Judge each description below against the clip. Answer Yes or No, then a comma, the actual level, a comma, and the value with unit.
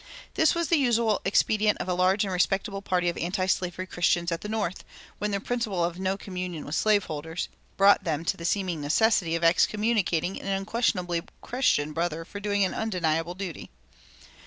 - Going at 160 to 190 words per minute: Yes, average, 180 wpm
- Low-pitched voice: No, medium, 185 Hz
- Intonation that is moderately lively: Yes, average, 3.4 semitones